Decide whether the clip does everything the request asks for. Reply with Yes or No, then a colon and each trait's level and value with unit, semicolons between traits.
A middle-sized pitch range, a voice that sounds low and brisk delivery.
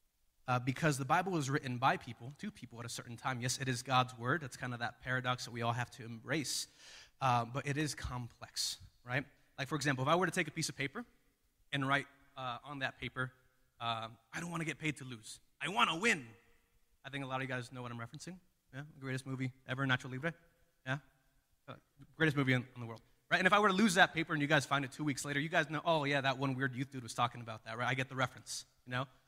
Yes: average, 3.0 semitones; low, 130 Hz; fast, 265 wpm